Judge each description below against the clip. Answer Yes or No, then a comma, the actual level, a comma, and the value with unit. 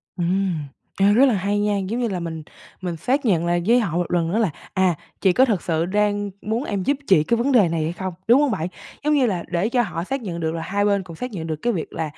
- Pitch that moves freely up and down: No, average, 4.9 semitones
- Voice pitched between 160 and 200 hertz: Yes, high, 195 Hz